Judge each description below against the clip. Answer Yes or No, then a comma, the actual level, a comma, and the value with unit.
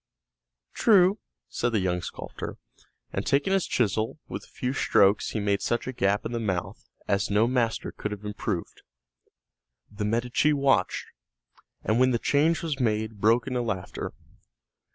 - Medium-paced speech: Yes, average, 155 wpm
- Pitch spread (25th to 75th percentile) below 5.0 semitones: Yes, average, 3.9 semitones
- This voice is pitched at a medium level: No, low, 115 Hz